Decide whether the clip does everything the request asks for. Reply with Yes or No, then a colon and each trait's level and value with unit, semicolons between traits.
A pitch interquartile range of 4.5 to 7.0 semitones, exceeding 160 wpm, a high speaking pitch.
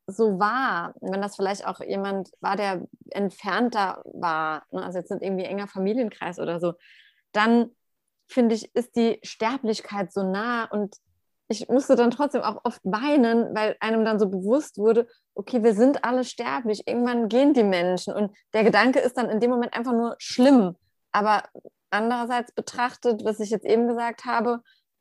No: average, 3.3 semitones; average, 170 wpm; high, 225 Hz